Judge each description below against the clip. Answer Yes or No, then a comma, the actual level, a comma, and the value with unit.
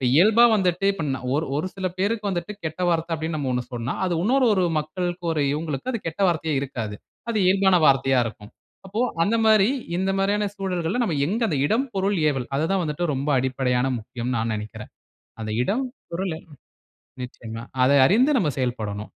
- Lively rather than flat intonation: Yes, wide, 6.9 semitones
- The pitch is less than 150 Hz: No, medium, 165 Hz